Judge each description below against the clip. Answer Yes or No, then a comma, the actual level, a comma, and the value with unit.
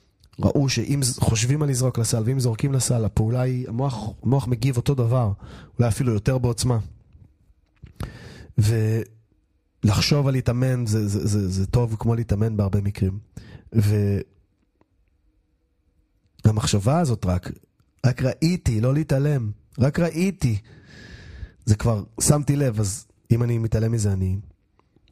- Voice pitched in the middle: No, low, 115 Hz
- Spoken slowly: No, average, 120 wpm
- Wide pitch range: No, average, 3.9 semitones